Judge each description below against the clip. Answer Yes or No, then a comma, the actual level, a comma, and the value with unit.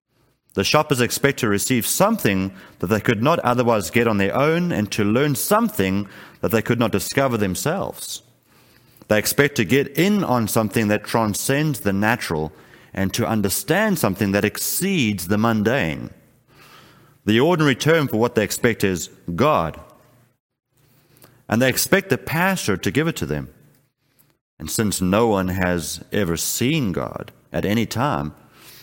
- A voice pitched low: Yes, low, 115 Hz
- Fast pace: No, average, 155 wpm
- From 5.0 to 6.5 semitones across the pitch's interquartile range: Yes, wide, 5.4 semitones